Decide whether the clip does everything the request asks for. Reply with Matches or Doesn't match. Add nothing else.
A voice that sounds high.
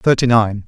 Doesn't match